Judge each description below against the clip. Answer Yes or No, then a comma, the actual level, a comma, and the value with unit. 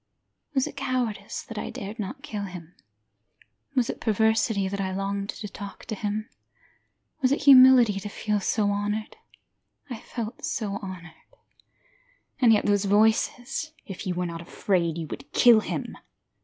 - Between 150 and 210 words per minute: Yes, average, 155 wpm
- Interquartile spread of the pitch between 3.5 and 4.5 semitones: No, narrow, 2.6 semitones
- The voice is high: Yes, high, 210 Hz